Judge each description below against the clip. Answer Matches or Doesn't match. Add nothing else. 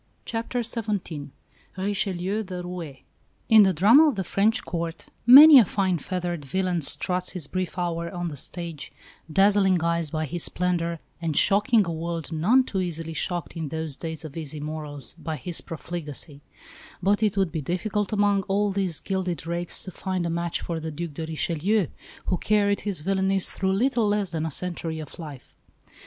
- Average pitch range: Matches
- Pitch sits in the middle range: Matches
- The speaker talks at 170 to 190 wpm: Matches